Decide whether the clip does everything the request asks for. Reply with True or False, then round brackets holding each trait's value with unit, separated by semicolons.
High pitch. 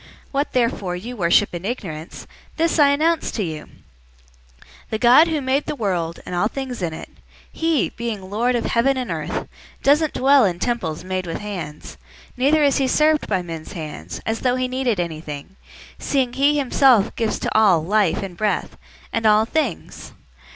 True (225 Hz)